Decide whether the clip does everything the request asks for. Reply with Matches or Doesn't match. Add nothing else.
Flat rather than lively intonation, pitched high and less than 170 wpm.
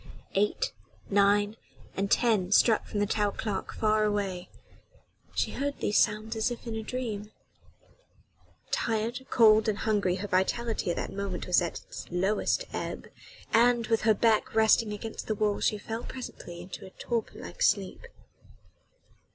Matches